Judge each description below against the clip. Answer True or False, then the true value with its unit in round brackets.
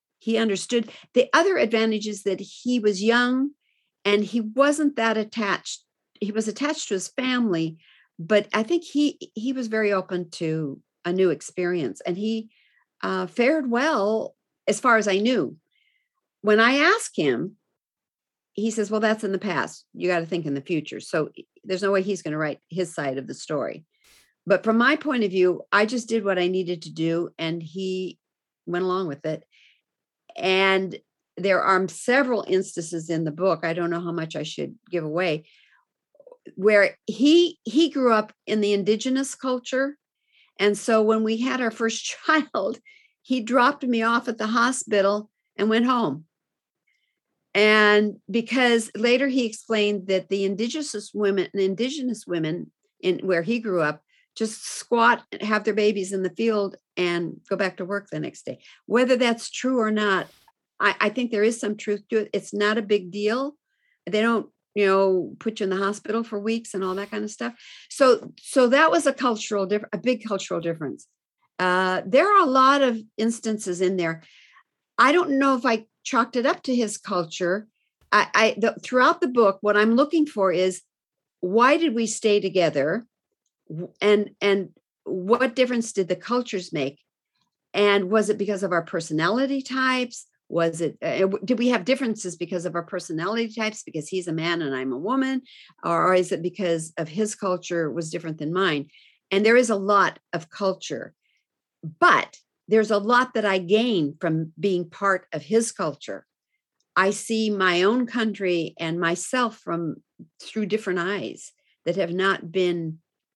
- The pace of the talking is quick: False (180 wpm)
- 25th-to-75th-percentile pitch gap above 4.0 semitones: True (4.7 semitones)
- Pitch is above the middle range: True (210 Hz)